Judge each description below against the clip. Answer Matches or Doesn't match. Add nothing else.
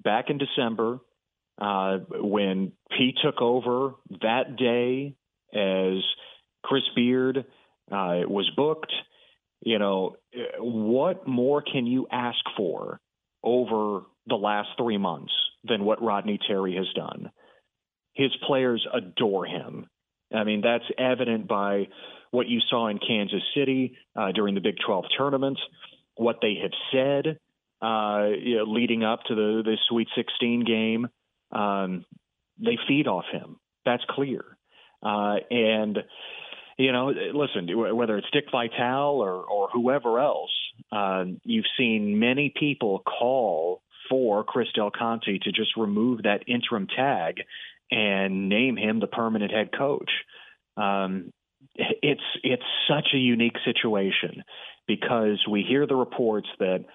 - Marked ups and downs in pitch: Doesn't match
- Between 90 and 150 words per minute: Matches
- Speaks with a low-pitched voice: Matches